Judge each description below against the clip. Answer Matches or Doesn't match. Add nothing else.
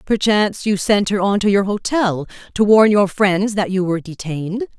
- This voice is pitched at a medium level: Doesn't match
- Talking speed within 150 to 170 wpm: Doesn't match